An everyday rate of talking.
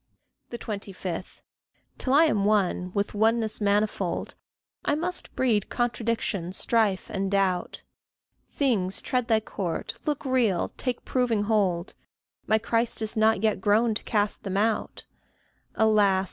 No: slow, 130 wpm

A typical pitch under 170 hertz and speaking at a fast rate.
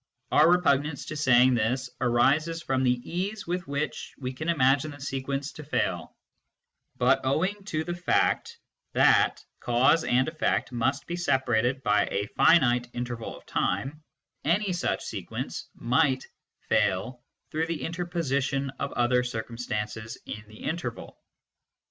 No: low, 135 Hz; average, 140 wpm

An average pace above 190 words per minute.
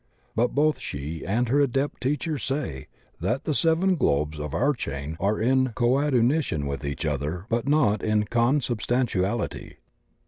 No: average, 145 wpm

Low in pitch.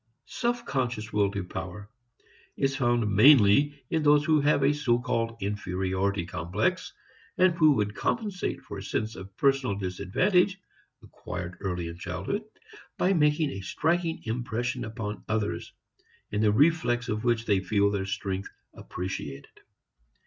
Yes: low, 110 Hz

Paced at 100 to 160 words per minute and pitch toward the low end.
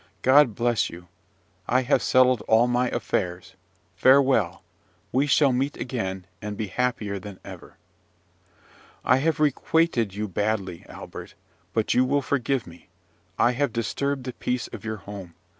Yes: average, 145 wpm; low, 120 Hz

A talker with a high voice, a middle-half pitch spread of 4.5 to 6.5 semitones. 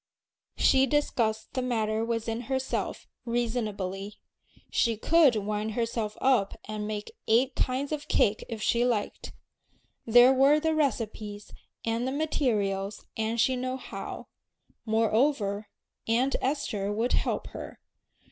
No: high, 230 Hz; average, 3.4 semitones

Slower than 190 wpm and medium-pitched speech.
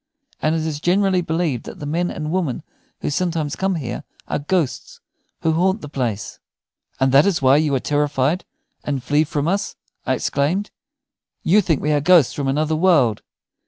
Yes: average, 180 wpm; medium, 155 Hz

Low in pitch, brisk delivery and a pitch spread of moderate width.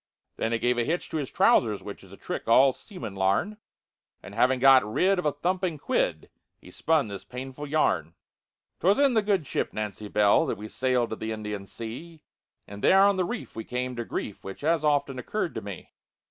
No: low, 130 Hz; fast, 210 wpm; wide, 7.2 semitones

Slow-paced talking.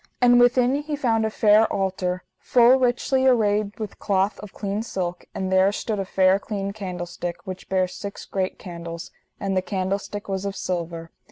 No: average, 175 wpm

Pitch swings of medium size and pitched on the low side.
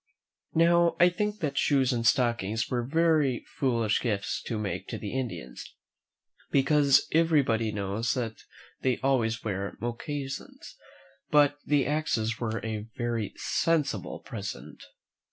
Yes: average, 4.6 semitones; low, 125 Hz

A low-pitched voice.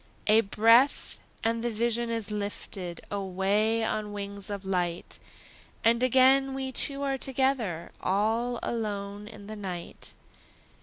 No: high, 215 Hz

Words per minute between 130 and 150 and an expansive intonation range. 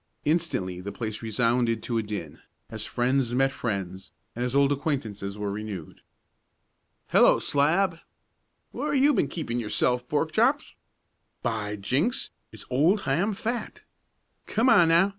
Yes: average, 140 wpm; wide, 7.5 semitones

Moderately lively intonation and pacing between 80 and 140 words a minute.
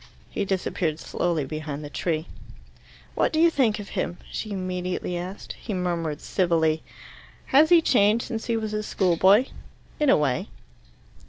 No: average, 4.9 semitones; average, 155 wpm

